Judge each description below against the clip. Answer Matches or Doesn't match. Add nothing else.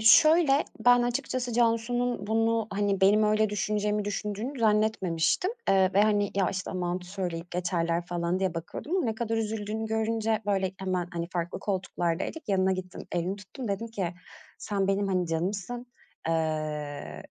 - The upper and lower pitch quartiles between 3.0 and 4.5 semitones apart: Matches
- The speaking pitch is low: Doesn't match